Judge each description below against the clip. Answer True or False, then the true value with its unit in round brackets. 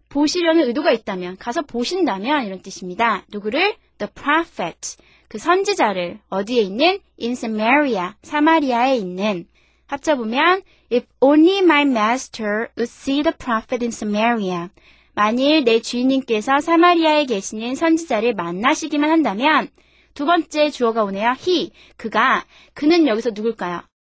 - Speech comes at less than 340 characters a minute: False (390 characters per minute)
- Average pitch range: False (6.2 semitones)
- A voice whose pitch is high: True (250 Hz)